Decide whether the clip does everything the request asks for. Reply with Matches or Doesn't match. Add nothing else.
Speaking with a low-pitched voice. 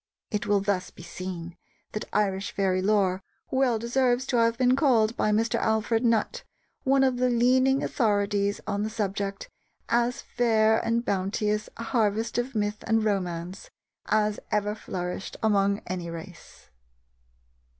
Doesn't match